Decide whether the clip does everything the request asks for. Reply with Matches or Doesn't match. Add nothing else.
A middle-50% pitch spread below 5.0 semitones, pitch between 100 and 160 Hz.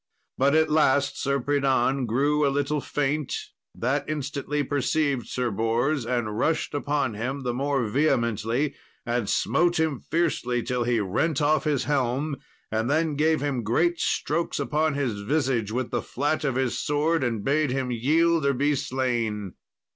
Matches